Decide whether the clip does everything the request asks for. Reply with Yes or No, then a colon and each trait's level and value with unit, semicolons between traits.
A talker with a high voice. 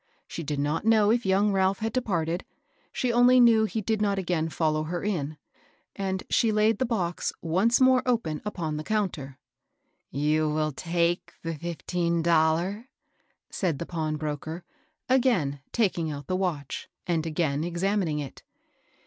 No: medium, 175 Hz